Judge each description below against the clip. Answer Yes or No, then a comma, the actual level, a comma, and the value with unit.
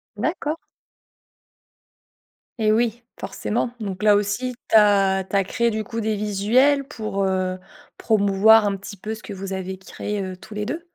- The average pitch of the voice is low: No, high, 210 Hz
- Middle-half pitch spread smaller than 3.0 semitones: Yes, narrow, 2.4 semitones